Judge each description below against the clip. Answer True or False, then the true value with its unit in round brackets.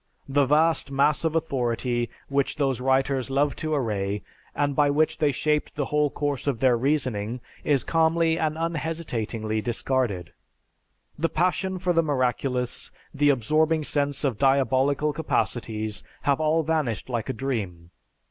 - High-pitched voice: False (140 Hz)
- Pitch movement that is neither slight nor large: True (3.8 semitones)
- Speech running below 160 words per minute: True (145 wpm)